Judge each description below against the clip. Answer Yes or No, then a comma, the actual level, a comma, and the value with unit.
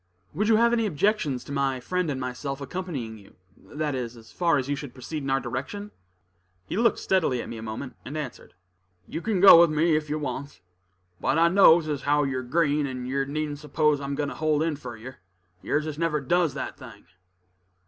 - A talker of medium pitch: Yes, medium, 145 Hz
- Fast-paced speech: Yes, fast, 215 wpm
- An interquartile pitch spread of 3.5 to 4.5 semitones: Yes, average, 4.0 semitones